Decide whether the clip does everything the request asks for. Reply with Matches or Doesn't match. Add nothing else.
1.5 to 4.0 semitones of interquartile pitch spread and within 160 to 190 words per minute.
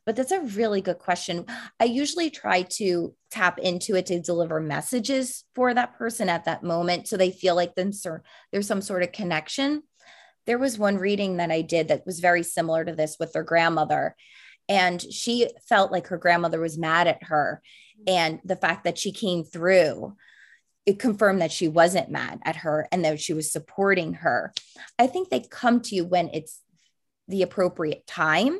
Doesn't match